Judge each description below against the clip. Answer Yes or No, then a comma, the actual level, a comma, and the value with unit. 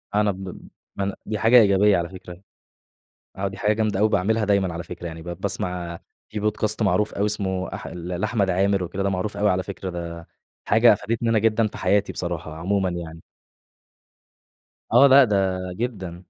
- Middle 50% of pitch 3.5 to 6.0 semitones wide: No, average, 2.9 semitones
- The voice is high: No, low, 100 Hz